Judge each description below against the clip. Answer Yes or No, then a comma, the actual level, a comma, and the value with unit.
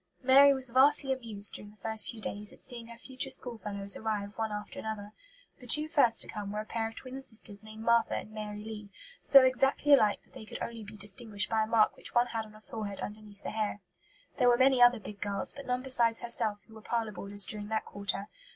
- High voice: Yes, high, 220 Hz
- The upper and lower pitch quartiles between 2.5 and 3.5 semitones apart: Yes, average, 2.8 semitones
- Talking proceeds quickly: Yes, fast, 235 wpm